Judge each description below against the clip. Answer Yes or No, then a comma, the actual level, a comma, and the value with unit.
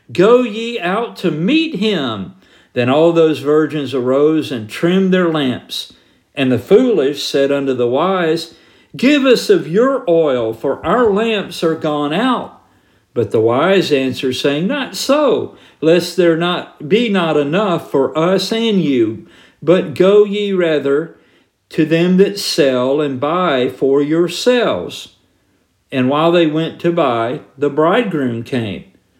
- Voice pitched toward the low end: No, medium, 165 Hz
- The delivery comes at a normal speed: Yes, average, 145 wpm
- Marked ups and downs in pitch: Yes, wide, 5.7 semitones